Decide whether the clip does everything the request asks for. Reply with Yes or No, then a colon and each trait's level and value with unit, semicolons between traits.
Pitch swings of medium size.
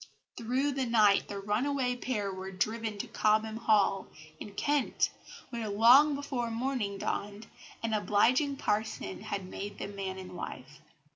Yes: average, 3.8 semitones